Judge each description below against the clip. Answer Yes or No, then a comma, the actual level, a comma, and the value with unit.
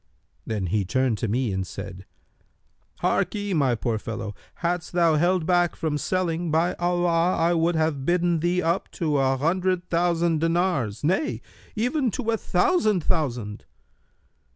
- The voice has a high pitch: No, medium, 165 Hz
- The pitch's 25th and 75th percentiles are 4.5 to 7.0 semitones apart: Yes, average, 5.1 semitones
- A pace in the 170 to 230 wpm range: No, average, 150 wpm